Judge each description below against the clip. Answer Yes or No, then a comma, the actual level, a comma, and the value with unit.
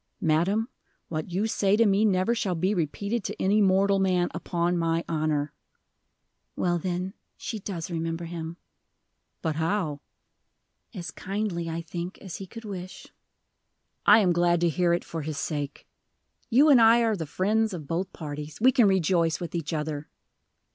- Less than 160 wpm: No, average, 165 wpm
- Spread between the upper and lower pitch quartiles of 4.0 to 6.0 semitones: No, average, 3.5 semitones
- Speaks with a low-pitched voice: No, medium, 175 Hz